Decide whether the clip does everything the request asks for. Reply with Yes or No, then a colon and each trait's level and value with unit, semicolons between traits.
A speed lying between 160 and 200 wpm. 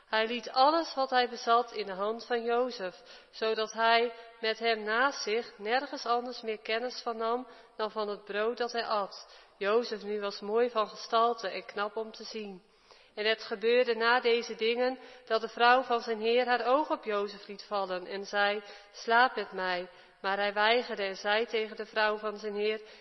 Yes: average, 195 wpm